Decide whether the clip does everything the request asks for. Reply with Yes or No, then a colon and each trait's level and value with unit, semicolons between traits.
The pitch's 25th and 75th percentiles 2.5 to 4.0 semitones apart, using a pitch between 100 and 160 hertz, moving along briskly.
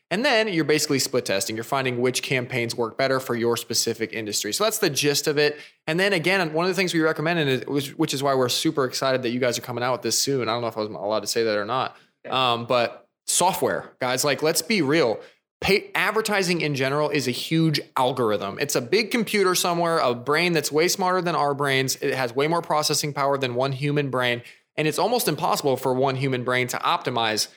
No: average, 4.5 semitones; medium, 140 Hz; fast, 235 wpm